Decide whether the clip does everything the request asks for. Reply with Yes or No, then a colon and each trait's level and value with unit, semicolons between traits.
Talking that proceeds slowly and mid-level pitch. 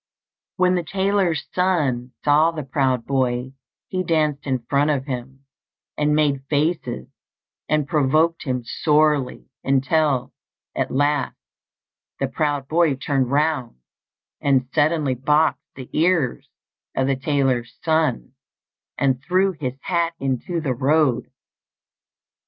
Yes: slow, 120 wpm; medium, 145 Hz